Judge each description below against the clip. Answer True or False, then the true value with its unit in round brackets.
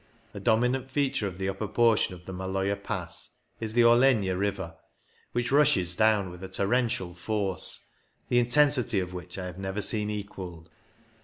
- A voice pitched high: False (100 Hz)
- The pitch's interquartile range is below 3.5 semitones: False (4.0 semitones)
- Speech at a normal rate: True (170 wpm)